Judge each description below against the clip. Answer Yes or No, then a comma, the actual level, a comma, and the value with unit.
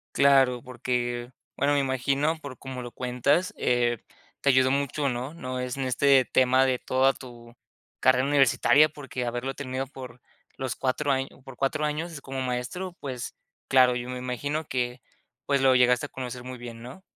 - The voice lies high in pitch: No, low, 130 Hz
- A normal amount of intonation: No, narrow, 1.9 semitones